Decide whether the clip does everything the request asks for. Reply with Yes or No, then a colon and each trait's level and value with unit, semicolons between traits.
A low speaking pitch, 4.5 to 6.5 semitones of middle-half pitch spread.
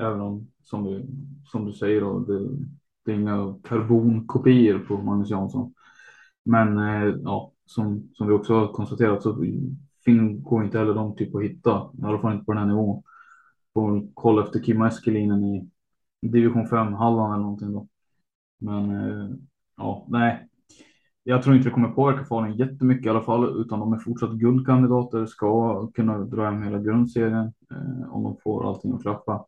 No: low, 110 Hz; narrow, 2.3 semitones